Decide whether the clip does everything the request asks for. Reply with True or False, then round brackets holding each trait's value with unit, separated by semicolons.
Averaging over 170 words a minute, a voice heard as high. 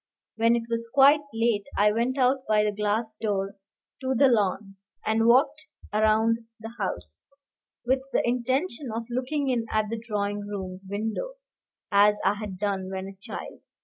False (165 wpm; 225 Hz)